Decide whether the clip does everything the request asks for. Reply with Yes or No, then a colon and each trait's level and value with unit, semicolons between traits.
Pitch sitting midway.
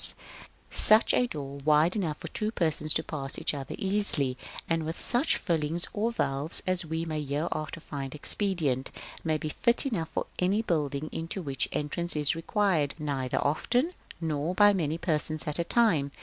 Yes: medium, 160 Hz